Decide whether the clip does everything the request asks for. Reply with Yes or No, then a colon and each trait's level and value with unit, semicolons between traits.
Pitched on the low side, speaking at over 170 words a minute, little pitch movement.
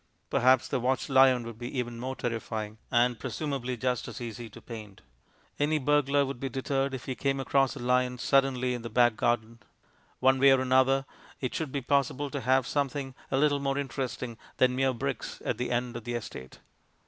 Yes: low, 130 Hz; average, 195 wpm; narrow, 2.2 semitones